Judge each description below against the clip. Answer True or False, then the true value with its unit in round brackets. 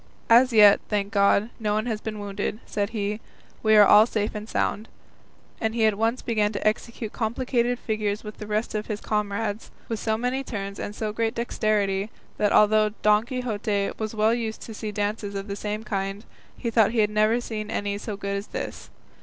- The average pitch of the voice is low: False (215 Hz)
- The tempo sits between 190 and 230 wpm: True (205 wpm)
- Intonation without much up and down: True (1.5 semitones)